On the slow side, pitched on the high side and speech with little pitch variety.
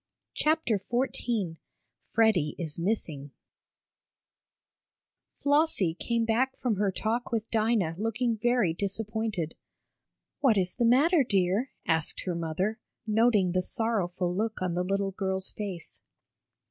No: slow, 120 wpm; high, 210 Hz; average, 4.4 semitones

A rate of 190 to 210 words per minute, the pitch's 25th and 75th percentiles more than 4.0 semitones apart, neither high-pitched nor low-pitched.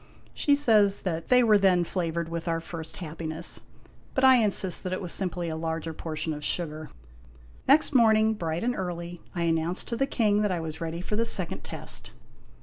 Yes: average, 195 wpm; average, 4.5 semitones; medium, 175 Hz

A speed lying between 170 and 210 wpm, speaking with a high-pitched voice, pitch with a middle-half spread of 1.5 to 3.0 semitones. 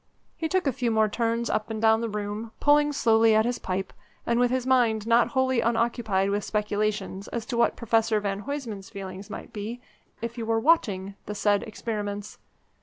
Yes: average, 190 wpm; high, 225 Hz; narrow, 2.4 semitones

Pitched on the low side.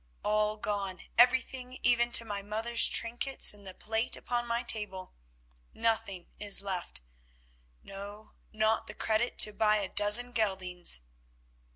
No: high, 215 Hz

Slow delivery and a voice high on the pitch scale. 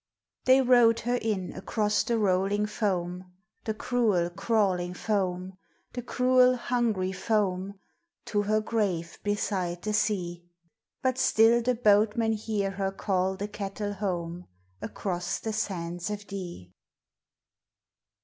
Yes: slow, 120 wpm; high, 205 Hz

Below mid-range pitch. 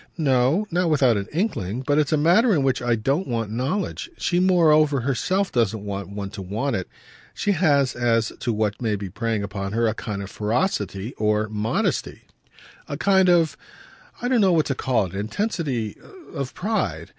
Yes: low, 125 Hz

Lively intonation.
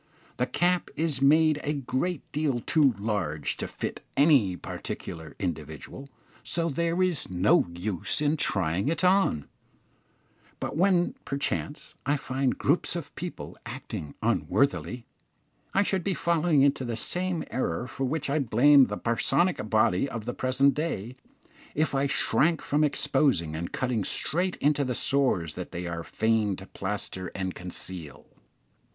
Yes: wide, 7.7 semitones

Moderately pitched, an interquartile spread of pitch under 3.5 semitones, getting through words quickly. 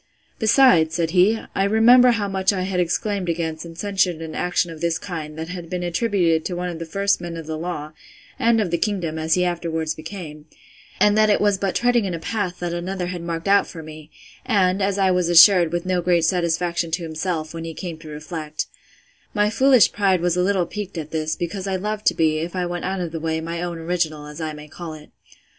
Yes: medium, 175 Hz; average, 3.1 semitones; fast, 235 wpm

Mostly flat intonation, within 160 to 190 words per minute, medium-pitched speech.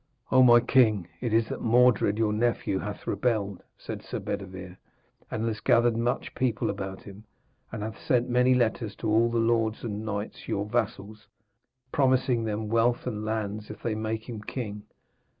No: narrow, 2.3 semitones; average, 170 wpm; low, 110 Hz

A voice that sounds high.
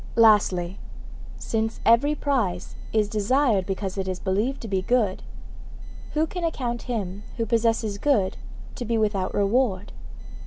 Yes: high, 220 Hz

